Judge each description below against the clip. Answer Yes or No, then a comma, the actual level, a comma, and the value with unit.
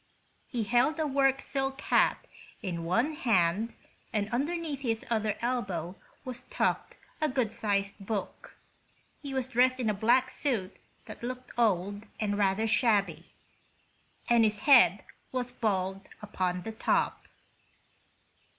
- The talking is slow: Yes, slow, 130 wpm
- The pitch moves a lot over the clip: No, average, 4.2 semitones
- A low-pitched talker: No, high, 225 Hz